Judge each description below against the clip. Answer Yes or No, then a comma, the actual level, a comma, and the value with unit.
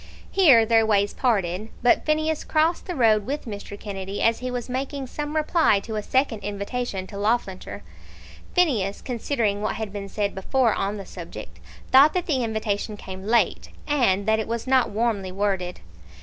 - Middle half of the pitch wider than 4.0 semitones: Yes, average, 4.5 semitones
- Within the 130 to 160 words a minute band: No, average, 175 wpm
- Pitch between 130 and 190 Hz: No, high, 220 Hz